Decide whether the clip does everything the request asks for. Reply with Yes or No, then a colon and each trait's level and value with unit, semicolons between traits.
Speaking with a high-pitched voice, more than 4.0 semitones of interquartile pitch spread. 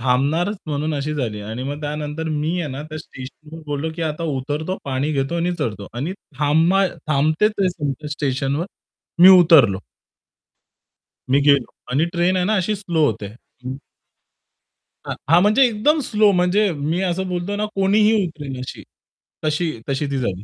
No: medium, 155 Hz; average, 4.4 semitones